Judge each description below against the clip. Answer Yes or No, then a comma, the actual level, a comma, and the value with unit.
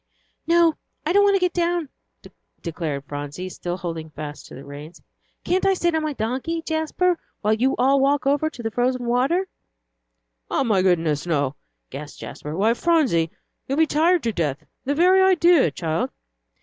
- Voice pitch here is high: Yes, very high, 255 Hz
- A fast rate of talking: No, average, 175 wpm